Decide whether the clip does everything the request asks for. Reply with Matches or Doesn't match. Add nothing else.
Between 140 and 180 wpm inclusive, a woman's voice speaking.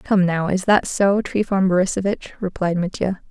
Matches